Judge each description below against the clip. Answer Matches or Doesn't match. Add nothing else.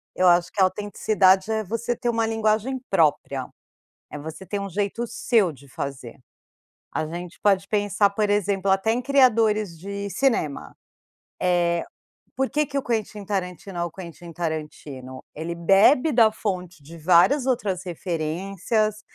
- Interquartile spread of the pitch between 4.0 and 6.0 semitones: Matches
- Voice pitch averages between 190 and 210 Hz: Matches